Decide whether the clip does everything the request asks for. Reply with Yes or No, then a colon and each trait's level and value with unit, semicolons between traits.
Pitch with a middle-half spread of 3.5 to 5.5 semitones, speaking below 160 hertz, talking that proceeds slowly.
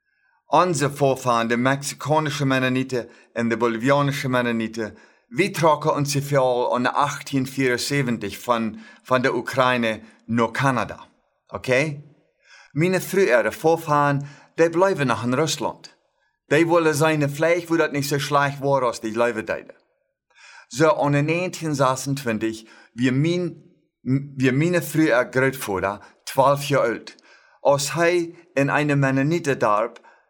Yes: average, 4.0 semitones; medium, 140 Hz; slow, 120 wpm